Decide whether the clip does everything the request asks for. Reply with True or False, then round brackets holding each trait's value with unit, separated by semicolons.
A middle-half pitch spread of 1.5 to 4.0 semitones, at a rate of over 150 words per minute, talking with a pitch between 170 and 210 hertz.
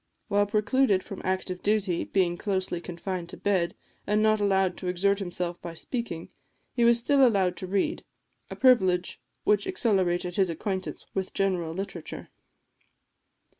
False (2.6 semitones; 145 wpm; 190 Hz)